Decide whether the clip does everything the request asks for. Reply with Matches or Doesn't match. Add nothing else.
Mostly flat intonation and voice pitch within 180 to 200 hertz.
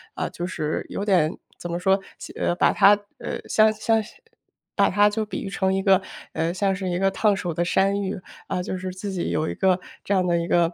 Matches